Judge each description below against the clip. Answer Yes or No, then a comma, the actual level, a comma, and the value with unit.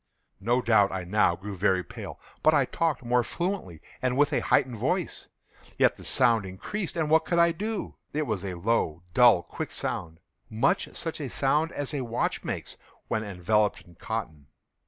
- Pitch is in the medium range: No, low, 115 Hz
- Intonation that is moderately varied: No, wide, 7.5 semitones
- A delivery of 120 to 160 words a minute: No, average, 170 wpm